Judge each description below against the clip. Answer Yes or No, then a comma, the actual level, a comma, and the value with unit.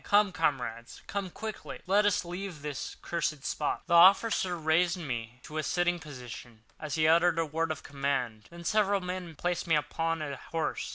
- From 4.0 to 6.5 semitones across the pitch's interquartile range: No, average, 3.5 semitones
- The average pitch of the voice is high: No, medium, 165 Hz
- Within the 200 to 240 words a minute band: No, average, 175 wpm